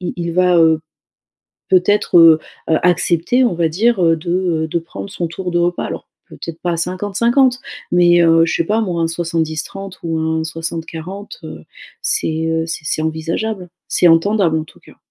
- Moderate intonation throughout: No, narrow, 2.3 semitones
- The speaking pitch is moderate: Yes, medium, 170 Hz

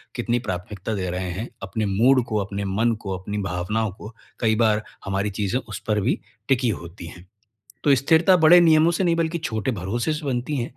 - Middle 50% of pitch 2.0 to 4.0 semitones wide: No, average, 5.3 semitones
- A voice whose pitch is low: Yes, low, 110 Hz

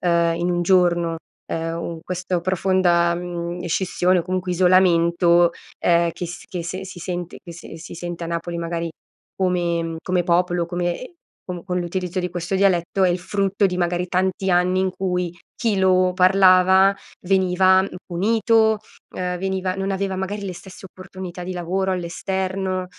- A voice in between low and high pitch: Yes, medium, 180 Hz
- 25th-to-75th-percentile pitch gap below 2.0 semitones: Yes, narrow, 1.5 semitones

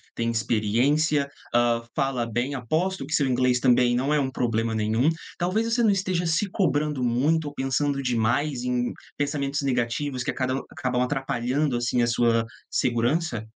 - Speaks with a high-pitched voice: No, low, 130 Hz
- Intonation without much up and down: No, average, 3.6 semitones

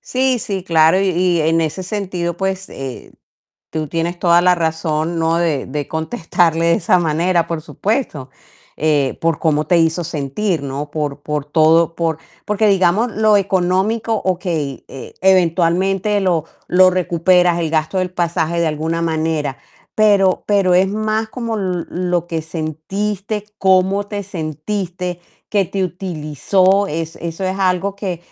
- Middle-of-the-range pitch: Yes, medium, 175 Hz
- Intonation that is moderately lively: Yes, average, 3.1 semitones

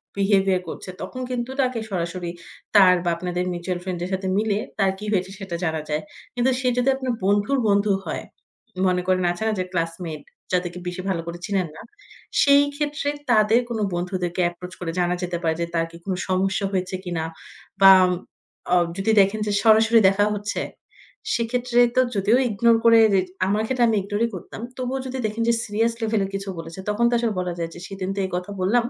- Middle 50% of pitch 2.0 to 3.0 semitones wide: No, average, 3.9 semitones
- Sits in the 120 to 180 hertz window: No, high, 195 Hz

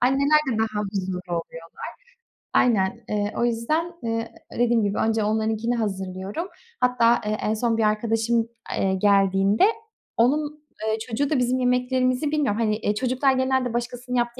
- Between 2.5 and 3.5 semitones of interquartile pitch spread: Yes, average, 3.0 semitones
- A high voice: Yes, high, 230 Hz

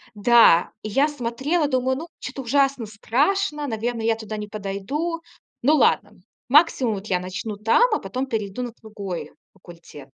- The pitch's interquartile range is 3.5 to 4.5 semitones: No, average, 5.3 semitones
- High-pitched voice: Yes, high, 235 Hz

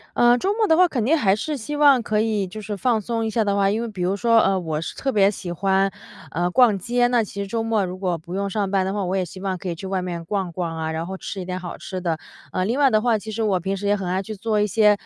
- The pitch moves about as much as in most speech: Yes, average, 3.5 semitones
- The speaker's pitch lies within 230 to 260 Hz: No, high, 200 Hz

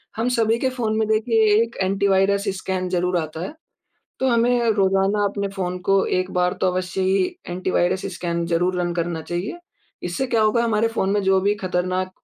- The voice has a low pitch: No, high, 195 Hz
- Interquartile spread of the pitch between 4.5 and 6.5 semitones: No, average, 3.1 semitones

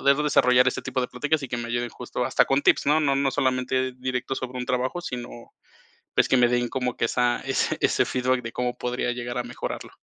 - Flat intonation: Yes, narrow, 1.3 semitones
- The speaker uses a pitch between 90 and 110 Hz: No, low, 125 Hz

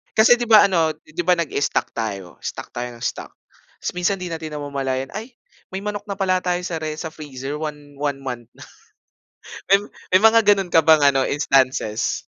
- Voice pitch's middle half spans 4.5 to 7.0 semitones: Yes, average, 5.2 semitones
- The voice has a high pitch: No, medium, 155 Hz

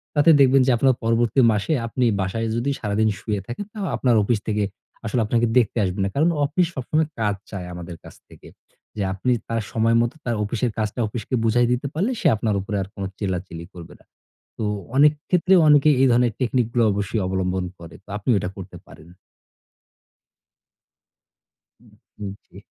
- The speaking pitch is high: No, low, 115 Hz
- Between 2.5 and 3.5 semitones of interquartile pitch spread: No, average, 4.2 semitones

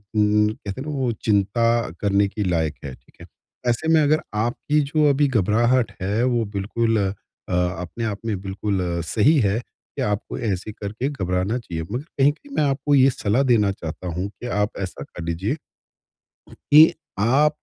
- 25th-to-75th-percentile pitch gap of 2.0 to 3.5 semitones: No, average, 5.1 semitones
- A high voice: No, low, 110 Hz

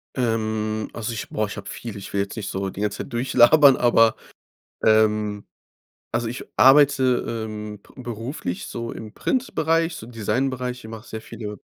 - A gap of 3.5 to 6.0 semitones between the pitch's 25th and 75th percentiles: No, average, 2.9 semitones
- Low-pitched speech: Yes, low, 115 Hz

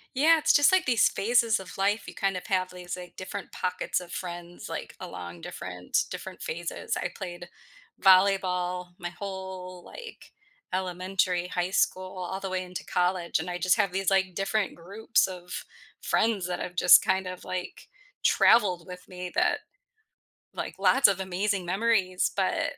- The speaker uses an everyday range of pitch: No, narrow, 1.5 semitones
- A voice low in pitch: No, medium, 185 Hz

